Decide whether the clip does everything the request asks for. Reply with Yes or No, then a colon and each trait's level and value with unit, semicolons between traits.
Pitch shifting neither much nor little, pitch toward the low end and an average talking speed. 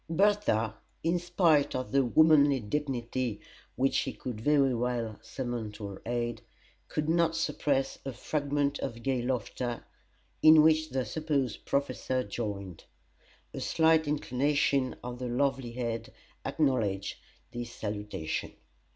No: average, 4.1 semitones; low, 130 Hz; slow, 125 wpm